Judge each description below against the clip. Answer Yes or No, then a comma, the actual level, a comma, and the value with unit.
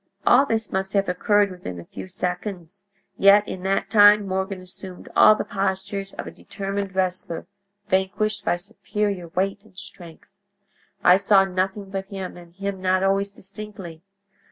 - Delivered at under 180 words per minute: Yes, average, 155 wpm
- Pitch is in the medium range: No, high, 195 Hz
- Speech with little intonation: Yes, narrow, 1.5 semitones